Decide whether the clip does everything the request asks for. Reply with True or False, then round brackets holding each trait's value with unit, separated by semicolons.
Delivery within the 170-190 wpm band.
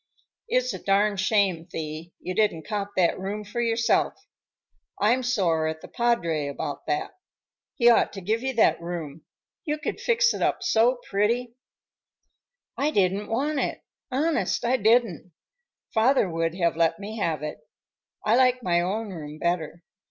False (160 wpm)